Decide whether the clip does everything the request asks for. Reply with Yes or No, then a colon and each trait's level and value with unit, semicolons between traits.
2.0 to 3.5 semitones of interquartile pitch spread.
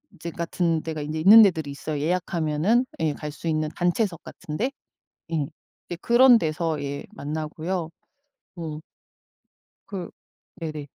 Yes: average, 2.8 semitones